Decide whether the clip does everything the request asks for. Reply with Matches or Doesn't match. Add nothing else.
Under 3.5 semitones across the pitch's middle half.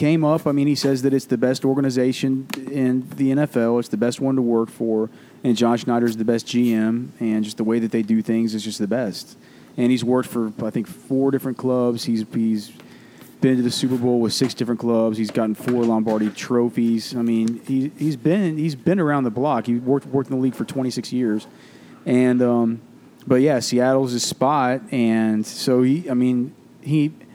Matches